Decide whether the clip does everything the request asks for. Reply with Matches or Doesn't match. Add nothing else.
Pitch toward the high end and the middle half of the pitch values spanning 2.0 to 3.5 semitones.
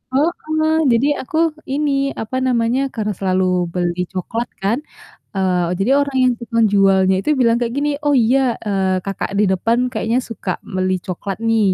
Doesn't match